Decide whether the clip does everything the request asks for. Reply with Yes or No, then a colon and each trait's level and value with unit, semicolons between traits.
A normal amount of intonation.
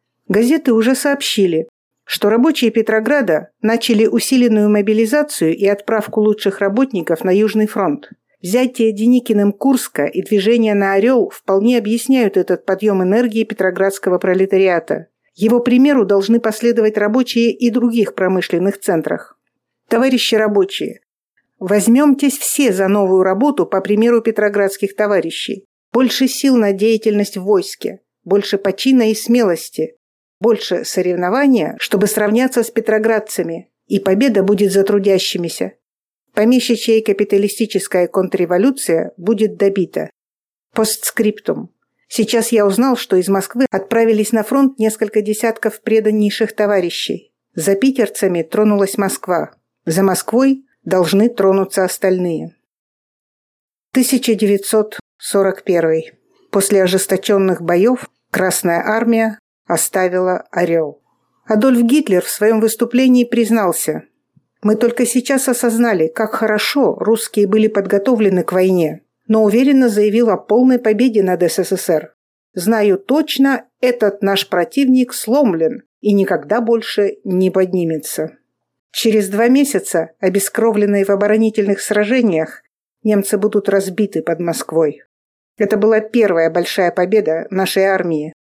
Yes: average, 3.3 semitones